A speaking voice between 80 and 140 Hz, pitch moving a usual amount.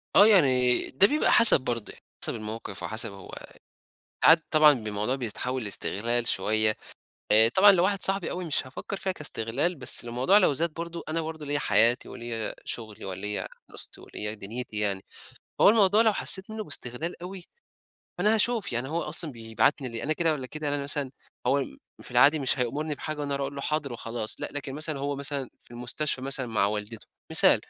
No: low, 135 Hz; wide, 5.8 semitones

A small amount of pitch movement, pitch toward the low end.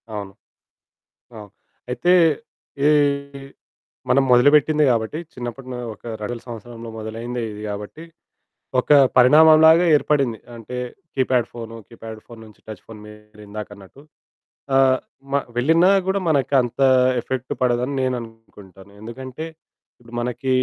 No: average, 3.4 semitones; low, 120 Hz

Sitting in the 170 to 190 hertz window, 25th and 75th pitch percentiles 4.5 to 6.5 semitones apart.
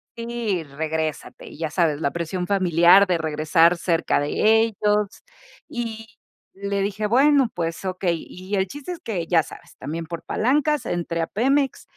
Yes: medium, 185 Hz; average, 5.1 semitones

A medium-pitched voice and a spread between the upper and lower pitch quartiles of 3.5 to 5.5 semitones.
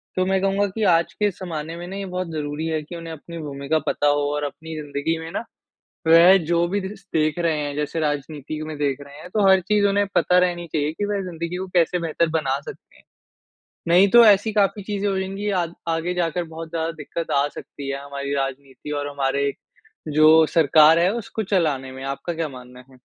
Yes: medium, 165 Hz; average, 4.1 semitones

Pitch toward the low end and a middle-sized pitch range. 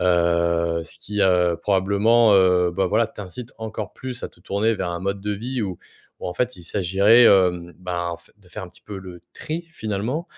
Yes: very low, 95 Hz; average, 3.8 semitones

